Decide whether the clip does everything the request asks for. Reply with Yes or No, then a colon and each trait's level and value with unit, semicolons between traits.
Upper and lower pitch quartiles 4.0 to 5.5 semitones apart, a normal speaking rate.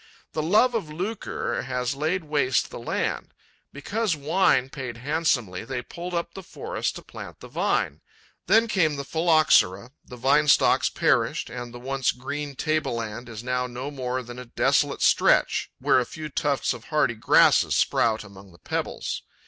Yes: average, 4.3 semitones; average, 170 wpm